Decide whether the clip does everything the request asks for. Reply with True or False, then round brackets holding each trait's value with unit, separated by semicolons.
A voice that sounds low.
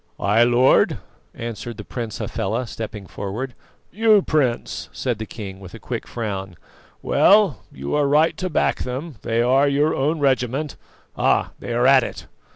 True (125 Hz)